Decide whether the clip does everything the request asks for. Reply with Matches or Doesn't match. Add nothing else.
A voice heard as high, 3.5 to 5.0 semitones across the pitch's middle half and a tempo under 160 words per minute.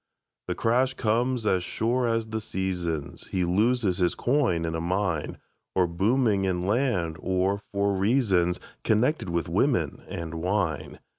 Doesn't match